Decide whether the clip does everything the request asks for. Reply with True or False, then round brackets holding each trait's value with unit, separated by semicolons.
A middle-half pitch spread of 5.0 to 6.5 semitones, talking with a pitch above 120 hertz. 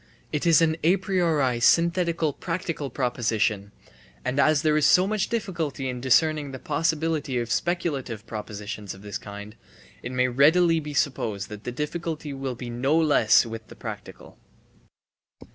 True (5.6 semitones; 140 Hz)